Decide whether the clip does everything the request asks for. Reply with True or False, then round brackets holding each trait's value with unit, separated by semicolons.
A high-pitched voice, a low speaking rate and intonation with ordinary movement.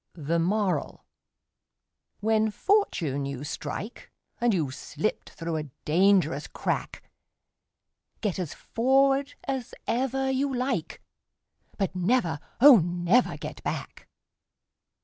False (200 Hz; 105 wpm; 7.5 semitones)